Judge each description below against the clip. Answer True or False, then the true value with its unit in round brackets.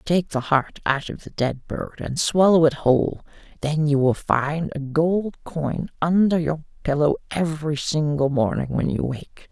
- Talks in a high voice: False (150 Hz)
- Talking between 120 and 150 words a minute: False (175 wpm)